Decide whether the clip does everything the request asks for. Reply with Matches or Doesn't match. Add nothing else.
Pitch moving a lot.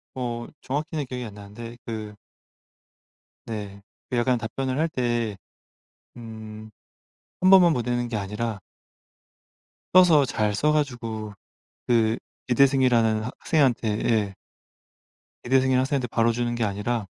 Doesn't match